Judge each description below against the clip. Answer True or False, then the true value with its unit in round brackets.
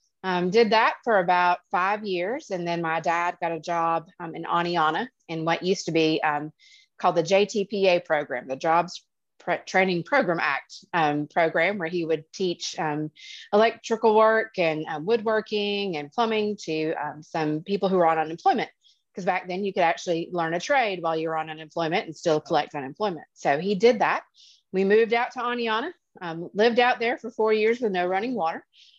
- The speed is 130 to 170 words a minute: False (195 wpm)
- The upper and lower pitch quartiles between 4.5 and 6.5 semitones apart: True (4.8 semitones)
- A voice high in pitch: False (180 Hz)